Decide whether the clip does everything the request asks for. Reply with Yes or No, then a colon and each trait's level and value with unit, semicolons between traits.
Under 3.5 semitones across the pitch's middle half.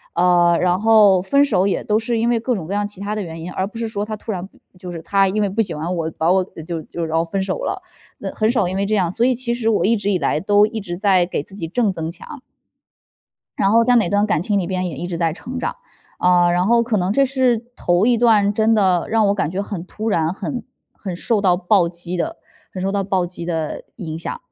No: average, 3.8 semitones